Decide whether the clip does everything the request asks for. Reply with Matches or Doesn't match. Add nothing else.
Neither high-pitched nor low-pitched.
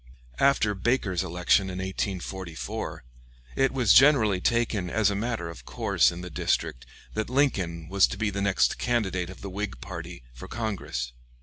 Doesn't match